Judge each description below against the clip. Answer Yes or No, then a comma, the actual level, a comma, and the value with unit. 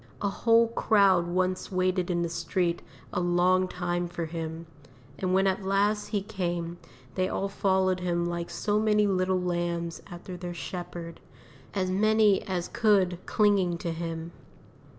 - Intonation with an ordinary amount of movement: No, narrow, 2.2 semitones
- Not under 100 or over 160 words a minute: Yes, average, 150 wpm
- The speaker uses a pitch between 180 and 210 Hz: Yes, medium, 185 Hz